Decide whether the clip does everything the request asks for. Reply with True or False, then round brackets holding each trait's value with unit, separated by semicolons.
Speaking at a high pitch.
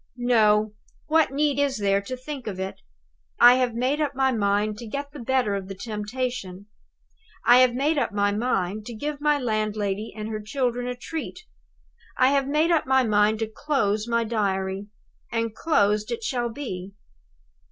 True (235 Hz)